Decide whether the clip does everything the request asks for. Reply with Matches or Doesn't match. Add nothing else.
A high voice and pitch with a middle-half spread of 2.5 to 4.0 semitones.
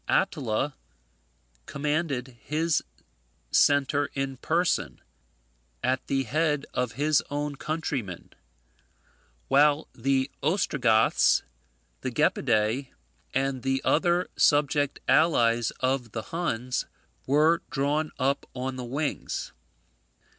Doesn't match